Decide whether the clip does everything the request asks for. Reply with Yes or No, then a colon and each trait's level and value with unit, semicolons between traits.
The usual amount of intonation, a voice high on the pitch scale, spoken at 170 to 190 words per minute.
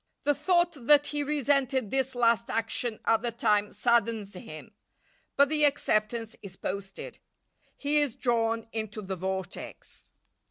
No: average, 4.9 semitones; high, 230 Hz; slow, 135 wpm